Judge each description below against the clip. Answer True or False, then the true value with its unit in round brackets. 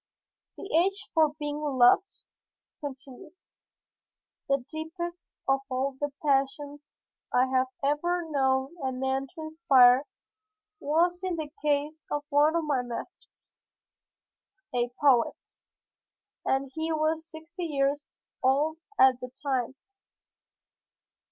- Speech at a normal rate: False (115 wpm)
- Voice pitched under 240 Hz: False (290 Hz)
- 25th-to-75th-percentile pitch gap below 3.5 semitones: True (3.1 semitones)